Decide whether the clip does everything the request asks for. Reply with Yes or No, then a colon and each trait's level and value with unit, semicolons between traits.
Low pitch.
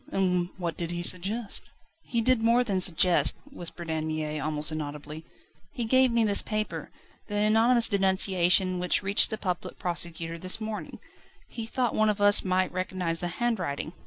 No: medium, 185 Hz